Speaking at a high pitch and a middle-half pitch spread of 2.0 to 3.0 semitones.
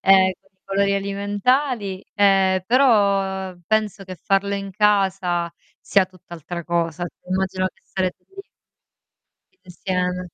No: high, 195 Hz; narrow, 1.5 semitones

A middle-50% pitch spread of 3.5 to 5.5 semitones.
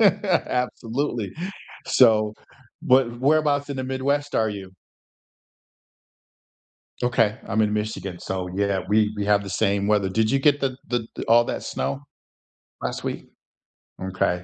Yes: average, 4.8 semitones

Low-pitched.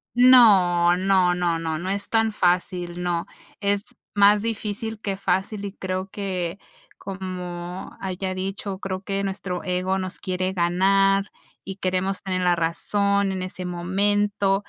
No: high, 190 Hz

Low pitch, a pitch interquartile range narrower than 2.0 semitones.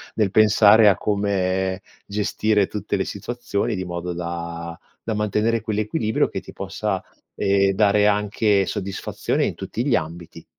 No: low, 100 Hz; narrow, 2.4 semitones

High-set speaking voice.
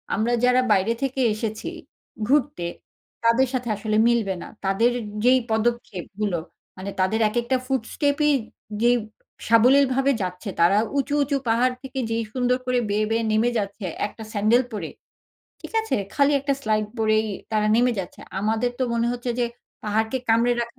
Yes: high, 230 Hz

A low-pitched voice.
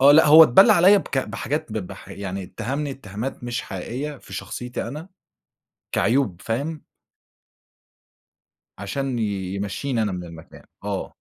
Yes: low, 125 Hz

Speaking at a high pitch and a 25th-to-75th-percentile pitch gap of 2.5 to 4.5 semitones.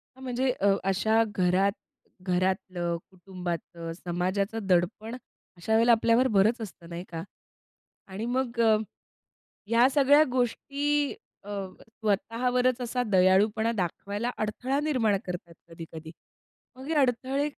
No: high, 215 Hz; average, 5.1 semitones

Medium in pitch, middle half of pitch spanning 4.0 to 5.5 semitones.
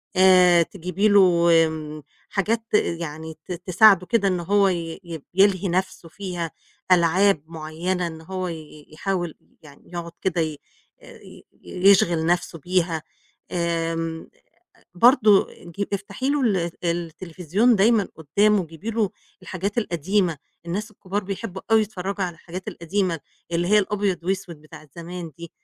No: medium, 180 Hz; average, 3.0 semitones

